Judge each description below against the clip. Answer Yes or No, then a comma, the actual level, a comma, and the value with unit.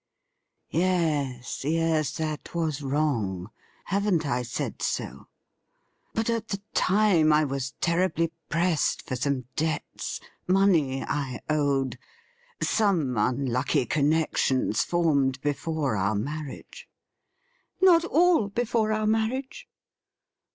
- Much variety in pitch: Yes, wide, 6.7 semitones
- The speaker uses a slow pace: Yes, slow, 115 wpm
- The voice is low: No, medium, 155 Hz